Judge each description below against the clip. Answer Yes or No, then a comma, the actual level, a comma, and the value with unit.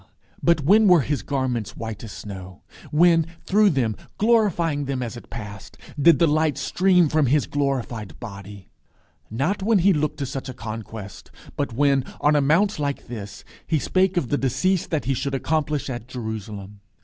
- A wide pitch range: Yes, wide, 6.2 semitones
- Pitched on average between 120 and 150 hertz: Yes, medium, 140 Hz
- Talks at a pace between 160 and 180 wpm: Yes, average, 175 wpm